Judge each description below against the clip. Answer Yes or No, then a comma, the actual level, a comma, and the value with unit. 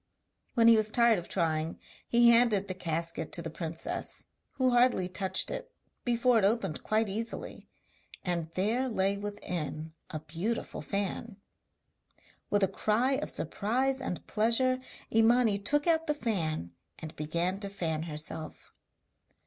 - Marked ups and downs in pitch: Yes, wide, 5.8 semitones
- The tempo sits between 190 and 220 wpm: No, average, 140 wpm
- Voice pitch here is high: Yes, high, 205 Hz